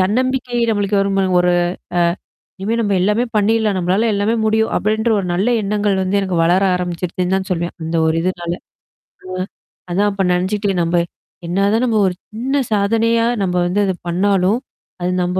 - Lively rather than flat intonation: No, average, 3.1 semitones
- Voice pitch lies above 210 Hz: No, high, 195 Hz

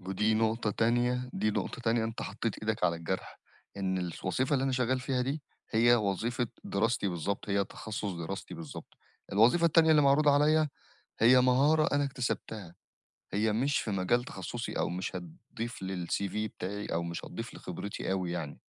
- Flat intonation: No, average, 4.8 semitones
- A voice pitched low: Yes, low, 110 Hz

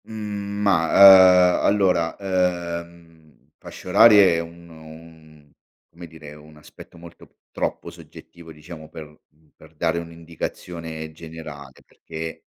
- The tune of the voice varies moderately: No, narrow, 2.3 semitones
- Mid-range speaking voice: No, very low, 85 Hz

